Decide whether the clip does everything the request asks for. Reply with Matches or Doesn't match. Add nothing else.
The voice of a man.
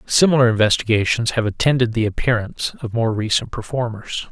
Matches